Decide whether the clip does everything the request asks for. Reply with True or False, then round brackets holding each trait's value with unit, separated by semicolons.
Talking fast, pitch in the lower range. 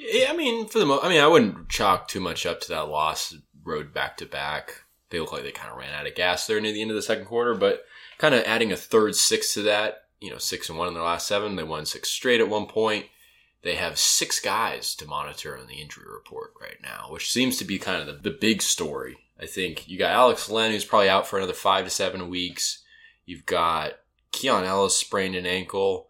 True (250 wpm; 110 Hz)